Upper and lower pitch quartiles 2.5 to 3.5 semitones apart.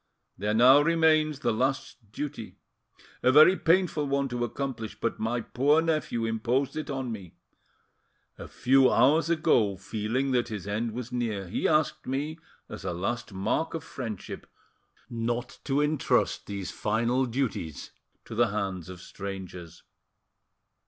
No: average, 4.7 semitones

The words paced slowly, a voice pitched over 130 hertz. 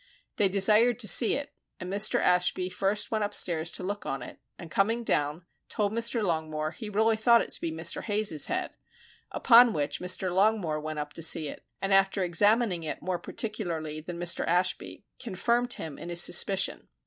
No: average, 185 wpm; high, 190 Hz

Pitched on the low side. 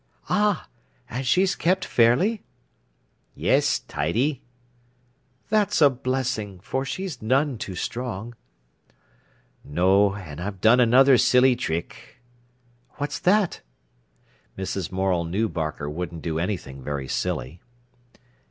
Yes: low, 115 Hz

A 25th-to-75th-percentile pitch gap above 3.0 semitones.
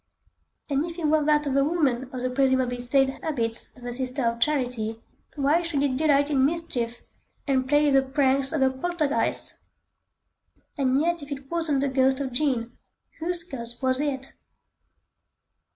No: narrow, 2.6 semitones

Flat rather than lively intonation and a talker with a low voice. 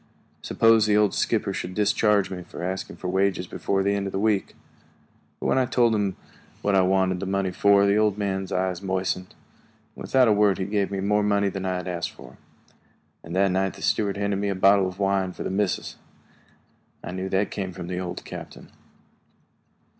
Yes: narrow, 1.6 semitones; very low, 95 Hz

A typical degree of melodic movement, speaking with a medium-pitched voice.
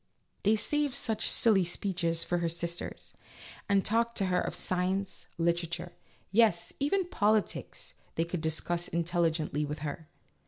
Yes: average, 3.8 semitones; medium, 175 Hz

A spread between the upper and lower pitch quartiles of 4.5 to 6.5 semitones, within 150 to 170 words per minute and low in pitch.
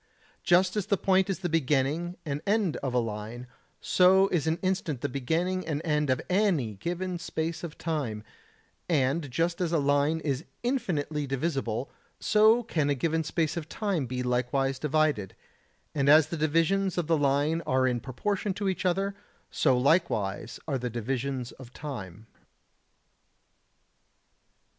No: average, 5.1 semitones; average, 155 wpm; medium, 155 Hz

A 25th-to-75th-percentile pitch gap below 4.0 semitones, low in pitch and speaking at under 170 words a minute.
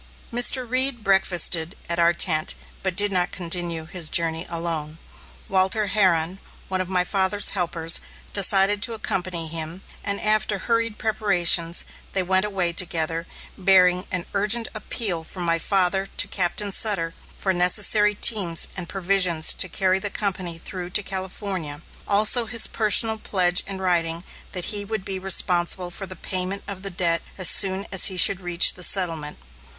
No: average, 2.7 semitones; medium, 185 Hz; average, 160 wpm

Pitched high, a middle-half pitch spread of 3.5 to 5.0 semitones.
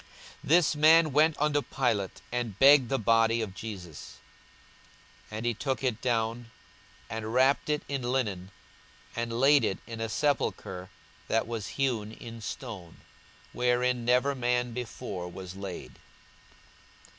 No: low, 120 Hz; average, 3.8 semitones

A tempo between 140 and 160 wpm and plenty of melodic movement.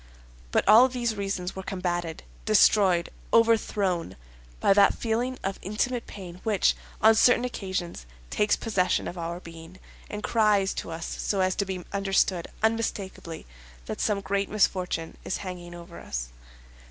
No: average, 145 wpm; average, 3.4 semitones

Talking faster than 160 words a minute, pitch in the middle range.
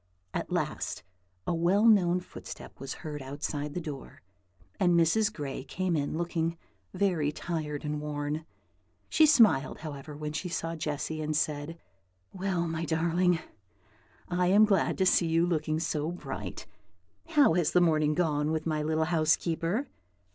No: average, 150 wpm; medium, 160 Hz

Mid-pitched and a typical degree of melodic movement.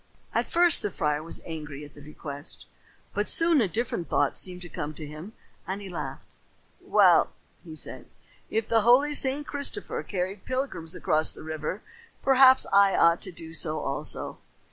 No: medium, 180 Hz; wide, 7.6 semitones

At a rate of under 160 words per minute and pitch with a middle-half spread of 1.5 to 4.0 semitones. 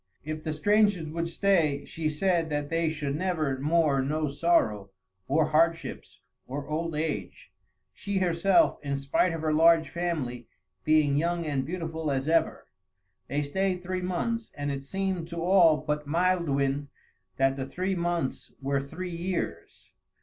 Yes: average, 150 wpm; average, 3.3 semitones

